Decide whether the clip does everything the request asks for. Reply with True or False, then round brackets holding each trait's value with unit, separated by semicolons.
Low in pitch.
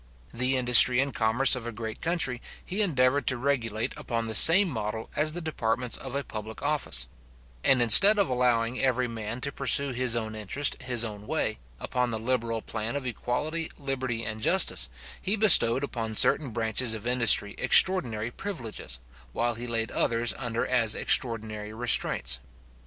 True (120 Hz)